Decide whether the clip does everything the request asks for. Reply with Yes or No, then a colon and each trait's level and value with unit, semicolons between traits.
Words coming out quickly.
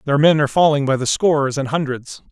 Yes: fast, 235 wpm